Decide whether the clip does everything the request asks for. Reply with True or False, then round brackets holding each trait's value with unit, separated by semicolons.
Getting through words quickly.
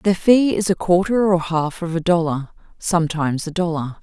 False (195 wpm)